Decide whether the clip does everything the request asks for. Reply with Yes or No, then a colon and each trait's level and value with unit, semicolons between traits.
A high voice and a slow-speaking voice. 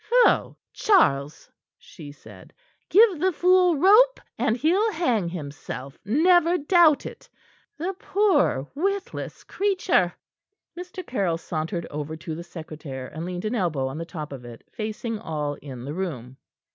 No: high, 195 Hz; average, 145 wpm